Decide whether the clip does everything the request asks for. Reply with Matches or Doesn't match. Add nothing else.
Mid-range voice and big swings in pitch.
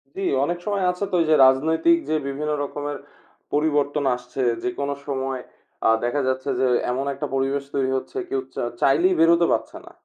Doesn't match